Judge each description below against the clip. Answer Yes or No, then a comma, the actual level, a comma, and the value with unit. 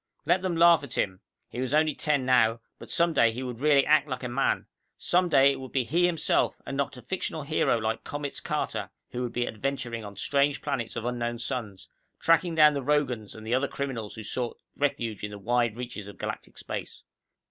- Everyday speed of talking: No, fast, 215 wpm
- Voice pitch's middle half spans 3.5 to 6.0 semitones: Yes, average, 4.0 semitones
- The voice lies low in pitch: Yes, low, 130 Hz